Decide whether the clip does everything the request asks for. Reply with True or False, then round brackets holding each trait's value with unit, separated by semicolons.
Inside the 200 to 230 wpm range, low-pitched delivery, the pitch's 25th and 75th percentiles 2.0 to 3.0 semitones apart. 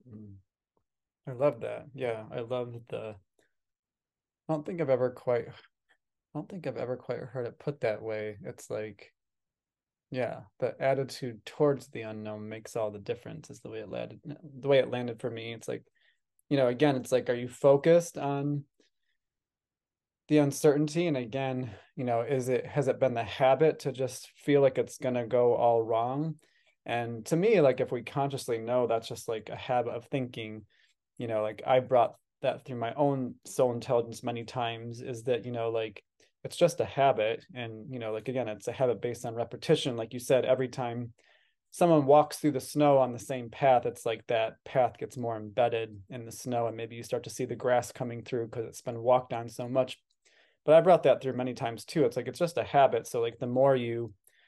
True (205 wpm; 125 Hz; 2.7 semitones)